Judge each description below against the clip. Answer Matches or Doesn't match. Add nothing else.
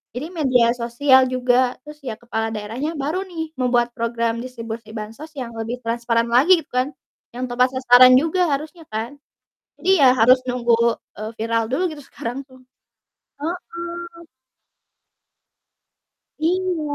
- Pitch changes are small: Doesn't match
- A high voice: Matches